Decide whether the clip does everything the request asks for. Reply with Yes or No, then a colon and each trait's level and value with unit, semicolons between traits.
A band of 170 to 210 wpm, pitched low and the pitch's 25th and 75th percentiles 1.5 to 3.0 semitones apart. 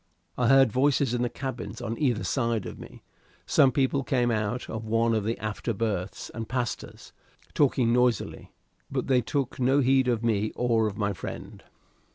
Yes: average, 185 wpm; low, 120 Hz; average, 2.7 semitones